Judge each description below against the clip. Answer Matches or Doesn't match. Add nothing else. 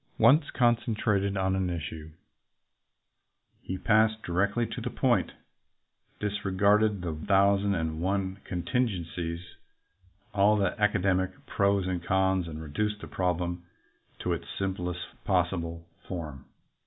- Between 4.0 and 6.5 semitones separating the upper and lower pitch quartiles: Doesn't match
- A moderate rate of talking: Doesn't match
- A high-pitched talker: Doesn't match